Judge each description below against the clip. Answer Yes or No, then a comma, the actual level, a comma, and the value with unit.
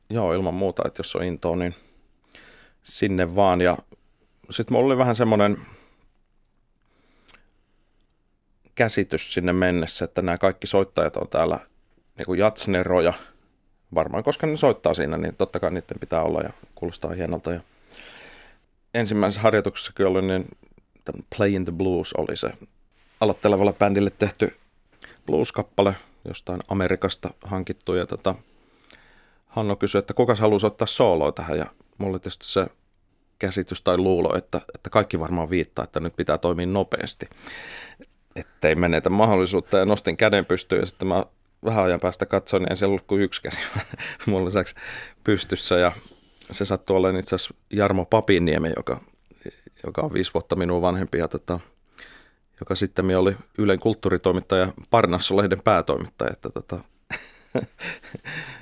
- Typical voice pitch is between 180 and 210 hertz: No, very low, 95 Hz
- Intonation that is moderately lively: No, narrow, 2.0 semitones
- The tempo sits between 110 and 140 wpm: Yes, average, 135 wpm